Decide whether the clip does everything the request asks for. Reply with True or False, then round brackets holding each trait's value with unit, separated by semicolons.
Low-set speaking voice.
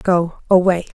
False (180 Hz)